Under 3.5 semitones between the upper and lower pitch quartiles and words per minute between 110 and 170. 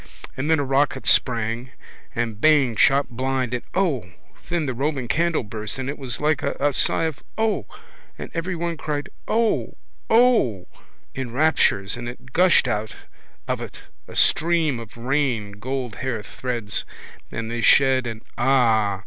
No: average, 4.8 semitones; average, 155 wpm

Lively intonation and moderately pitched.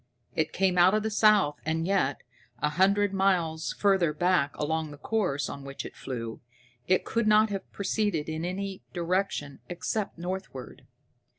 No: average, 4.5 semitones; medium, 180 Hz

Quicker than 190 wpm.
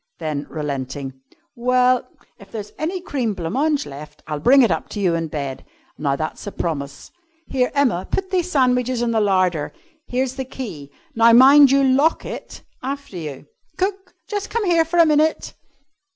No: average, 175 wpm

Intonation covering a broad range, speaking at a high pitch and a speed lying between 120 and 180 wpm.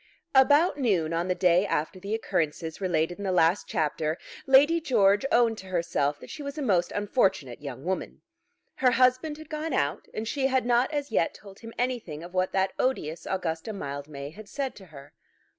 No: wide, 7.7 semitones; high, 195 Hz; average, 195 wpm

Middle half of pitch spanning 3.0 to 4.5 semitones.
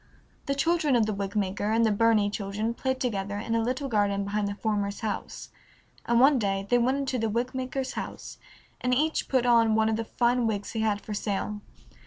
Yes: average, 3.5 semitones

